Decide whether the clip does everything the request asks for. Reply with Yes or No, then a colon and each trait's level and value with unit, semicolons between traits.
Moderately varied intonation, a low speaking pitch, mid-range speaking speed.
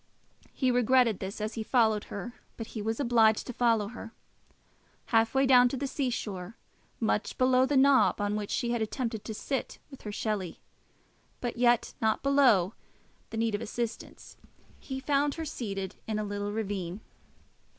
No: average, 3.3 semitones; high, 225 Hz; average, 170 wpm